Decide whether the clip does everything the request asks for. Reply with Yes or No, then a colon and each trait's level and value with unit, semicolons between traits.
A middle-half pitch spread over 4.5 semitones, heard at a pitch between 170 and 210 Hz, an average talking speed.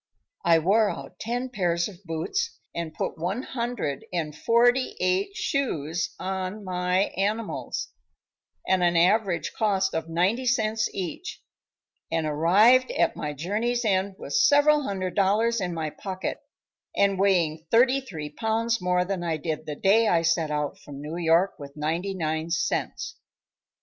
Yes: average, 5.1 semitones; medium, 185 Hz; average, 150 wpm